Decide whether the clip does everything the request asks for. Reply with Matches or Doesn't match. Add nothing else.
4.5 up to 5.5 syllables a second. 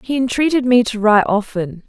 Doesn't match